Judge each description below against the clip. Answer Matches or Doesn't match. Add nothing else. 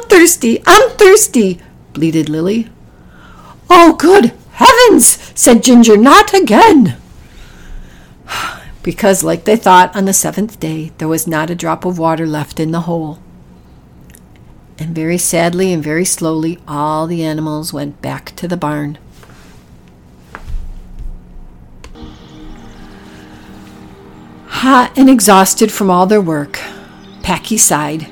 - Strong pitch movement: Matches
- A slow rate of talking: Matches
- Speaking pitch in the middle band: Matches